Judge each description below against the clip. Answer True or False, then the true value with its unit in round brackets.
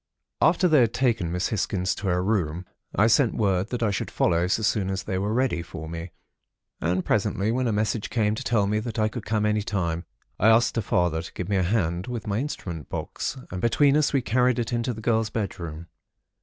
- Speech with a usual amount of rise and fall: True (4.3 semitones)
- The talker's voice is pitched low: True (105 Hz)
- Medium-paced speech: False (225 wpm)